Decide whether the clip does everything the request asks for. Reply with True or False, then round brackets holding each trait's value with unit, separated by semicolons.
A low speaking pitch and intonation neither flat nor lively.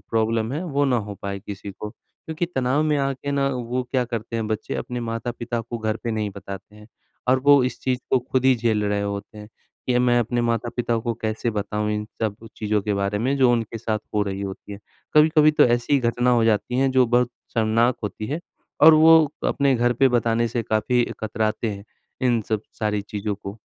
True (115 Hz; 3.1 semitones)